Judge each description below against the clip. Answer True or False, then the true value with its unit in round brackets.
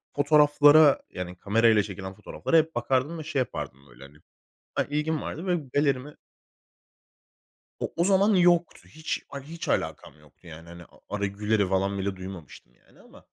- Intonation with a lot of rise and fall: True (8.6 semitones)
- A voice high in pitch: False (125 Hz)